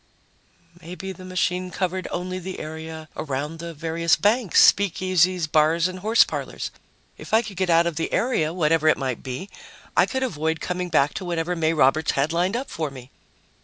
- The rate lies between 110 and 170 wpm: No, average, 185 wpm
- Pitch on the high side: No, medium, 170 Hz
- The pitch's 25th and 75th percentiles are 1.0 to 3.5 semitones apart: Yes, average, 2.8 semitones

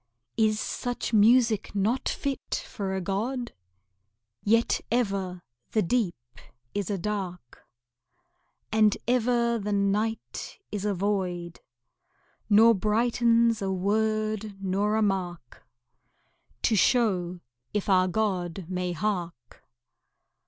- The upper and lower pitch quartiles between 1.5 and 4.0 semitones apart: Yes, average, 3.1 semitones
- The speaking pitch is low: No, high, 205 Hz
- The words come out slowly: Yes, slow, 105 wpm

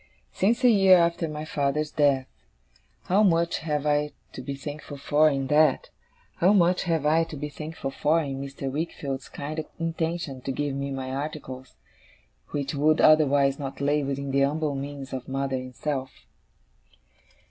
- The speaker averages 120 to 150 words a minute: No, average, 165 wpm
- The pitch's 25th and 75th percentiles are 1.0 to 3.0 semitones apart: Yes, narrow, 2.5 semitones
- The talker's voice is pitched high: No, medium, 145 Hz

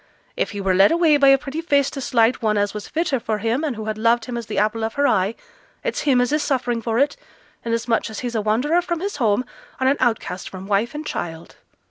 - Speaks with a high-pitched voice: Yes, high, 235 Hz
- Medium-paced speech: No, fast, 250 wpm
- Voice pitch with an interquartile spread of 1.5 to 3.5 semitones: No, average, 4.6 semitones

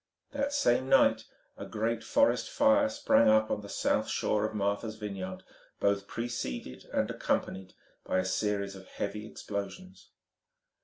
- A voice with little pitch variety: No, average, 3.4 semitones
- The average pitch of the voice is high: No, low, 105 Hz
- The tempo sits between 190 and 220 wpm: No, average, 145 wpm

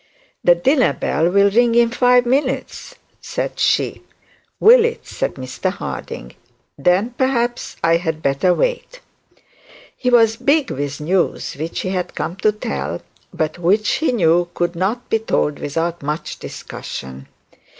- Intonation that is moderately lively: No, wide, 6.9 semitones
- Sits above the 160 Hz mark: Yes, high, 190 Hz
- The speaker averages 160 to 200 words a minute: No, average, 145 wpm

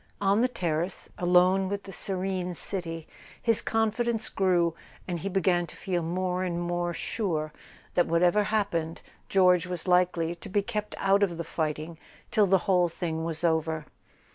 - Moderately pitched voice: Yes, medium, 180 Hz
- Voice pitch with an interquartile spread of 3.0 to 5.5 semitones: No, narrow, 2.6 semitones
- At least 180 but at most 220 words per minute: No, average, 165 wpm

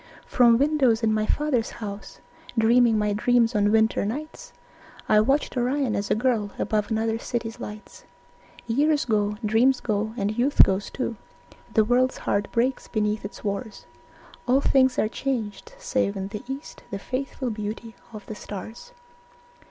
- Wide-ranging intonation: No, average, 3.5 semitones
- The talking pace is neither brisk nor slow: Yes, average, 155 wpm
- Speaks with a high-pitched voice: Yes, high, 225 Hz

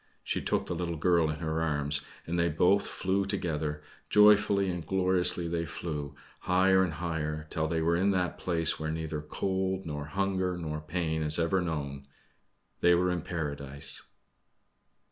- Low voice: Yes, very low, 85 Hz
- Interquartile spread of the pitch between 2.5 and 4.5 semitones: Yes, average, 3.0 semitones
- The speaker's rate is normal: Yes, average, 165 wpm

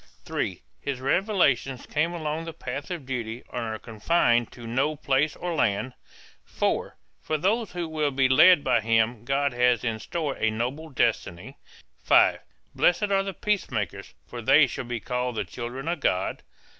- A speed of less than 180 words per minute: Yes, average, 170 wpm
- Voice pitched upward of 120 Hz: Yes, low, 135 Hz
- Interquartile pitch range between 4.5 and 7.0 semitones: Yes, average, 5.2 semitones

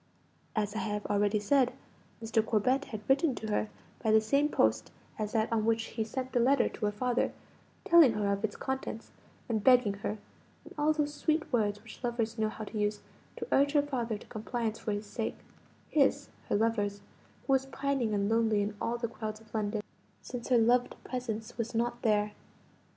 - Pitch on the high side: Yes, high, 225 Hz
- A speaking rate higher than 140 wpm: Yes, average, 195 wpm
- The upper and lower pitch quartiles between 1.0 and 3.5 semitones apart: Yes, average, 3.0 semitones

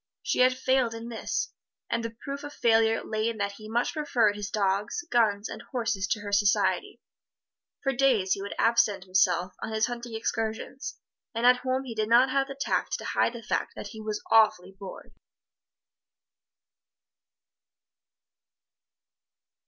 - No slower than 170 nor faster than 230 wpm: No, average, 160 wpm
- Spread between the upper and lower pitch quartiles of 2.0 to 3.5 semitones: Yes, average, 3.1 semitones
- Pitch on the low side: No, high, 225 Hz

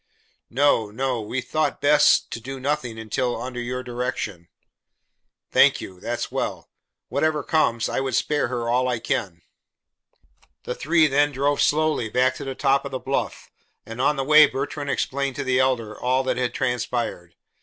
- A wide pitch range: No, average, 2.8 semitones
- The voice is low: Yes, low, 130 Hz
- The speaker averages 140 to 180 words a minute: Yes, average, 170 wpm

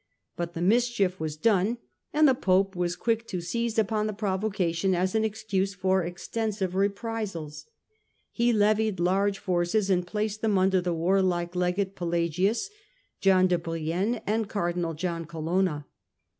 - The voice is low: No, high, 190 Hz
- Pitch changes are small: No, average, 3.6 semitones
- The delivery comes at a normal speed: Yes, average, 145 wpm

